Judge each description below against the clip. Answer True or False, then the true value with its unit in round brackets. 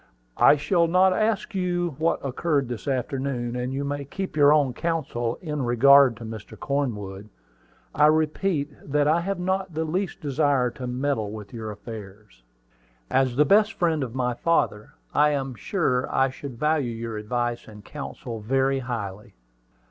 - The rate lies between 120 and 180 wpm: True (165 wpm)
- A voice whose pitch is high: False (135 Hz)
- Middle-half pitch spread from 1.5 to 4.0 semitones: False (4.6 semitones)